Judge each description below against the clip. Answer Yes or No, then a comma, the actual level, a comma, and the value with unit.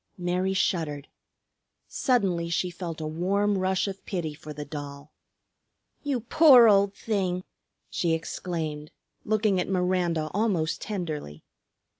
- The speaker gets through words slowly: Yes, slow, 120 wpm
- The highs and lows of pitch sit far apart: No, average, 4.0 semitones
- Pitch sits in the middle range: Yes, medium, 180 Hz